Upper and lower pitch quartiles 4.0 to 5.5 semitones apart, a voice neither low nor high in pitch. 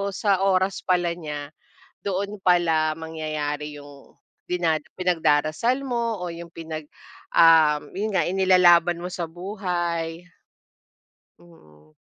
No: average, 3.0 semitones; medium, 170 Hz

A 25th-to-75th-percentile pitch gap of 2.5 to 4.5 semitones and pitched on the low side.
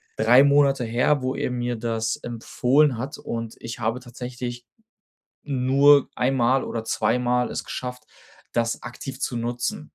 No: narrow, 1.8 semitones; low, 125 Hz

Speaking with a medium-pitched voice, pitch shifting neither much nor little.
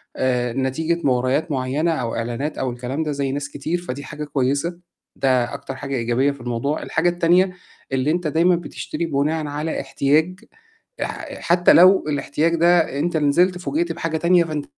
Yes: medium, 150 Hz; average, 4.1 semitones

